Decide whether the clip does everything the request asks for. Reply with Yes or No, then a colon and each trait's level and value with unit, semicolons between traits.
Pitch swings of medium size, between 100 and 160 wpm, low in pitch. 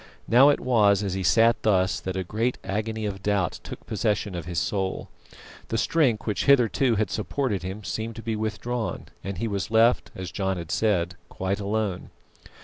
No: average, 3.0 semitones; average, 185 wpm; low, 105 Hz